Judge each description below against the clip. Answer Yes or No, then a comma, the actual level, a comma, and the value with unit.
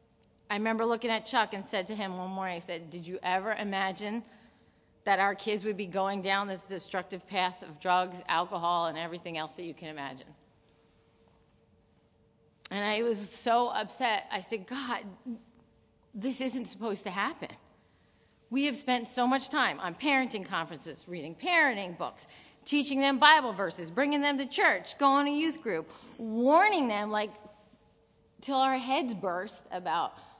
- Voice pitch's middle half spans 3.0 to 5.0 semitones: No, wide, 5.6 semitones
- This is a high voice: Yes, high, 210 Hz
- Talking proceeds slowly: No, average, 160 wpm